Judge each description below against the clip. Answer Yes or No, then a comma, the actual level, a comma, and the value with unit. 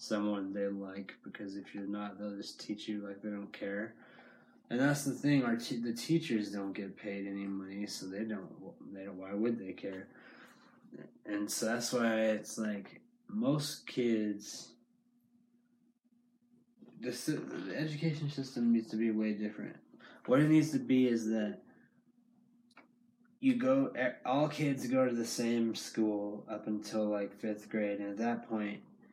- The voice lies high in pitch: No, low, 115 Hz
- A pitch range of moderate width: No, wide, 7.7 semitones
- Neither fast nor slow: Yes, average, 165 wpm